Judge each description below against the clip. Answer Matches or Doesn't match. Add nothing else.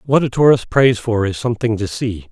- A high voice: Doesn't match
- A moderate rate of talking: Doesn't match